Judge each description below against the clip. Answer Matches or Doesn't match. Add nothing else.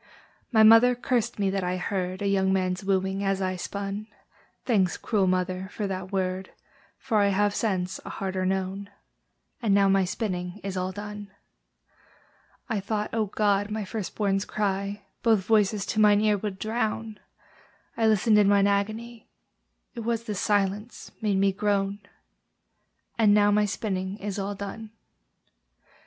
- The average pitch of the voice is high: Matches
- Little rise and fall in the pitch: Matches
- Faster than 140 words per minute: Matches